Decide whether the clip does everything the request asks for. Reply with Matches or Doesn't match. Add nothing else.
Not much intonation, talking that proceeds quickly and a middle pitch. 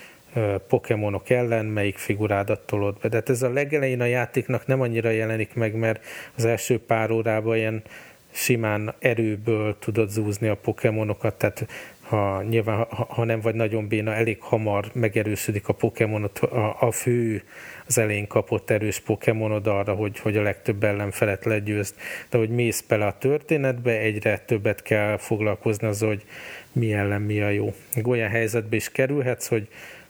Doesn't match